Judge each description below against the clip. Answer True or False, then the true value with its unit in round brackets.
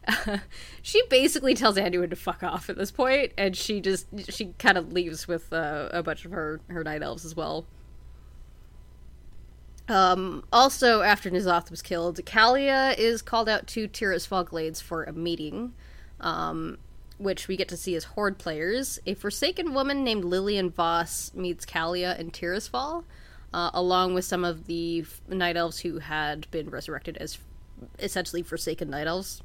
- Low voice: False (180 Hz)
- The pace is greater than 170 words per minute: False (165 wpm)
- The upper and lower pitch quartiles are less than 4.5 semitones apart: True (3.8 semitones)